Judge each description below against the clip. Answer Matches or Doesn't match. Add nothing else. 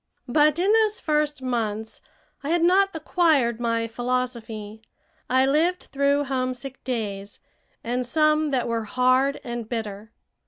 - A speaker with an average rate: Doesn't match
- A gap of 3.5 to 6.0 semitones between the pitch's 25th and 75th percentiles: Matches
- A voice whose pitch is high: Matches